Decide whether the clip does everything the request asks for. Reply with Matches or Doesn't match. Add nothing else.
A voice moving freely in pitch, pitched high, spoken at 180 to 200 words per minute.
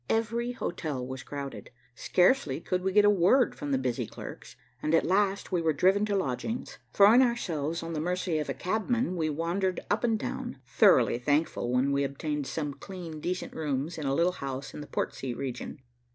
Doesn't match